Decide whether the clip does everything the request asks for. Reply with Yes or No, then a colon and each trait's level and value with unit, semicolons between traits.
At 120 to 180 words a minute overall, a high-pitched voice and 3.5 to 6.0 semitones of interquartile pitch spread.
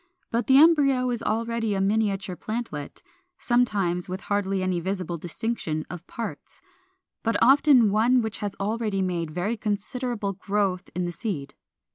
Yes: average, 145 wpm; high, 205 Hz; average, 4.1 semitones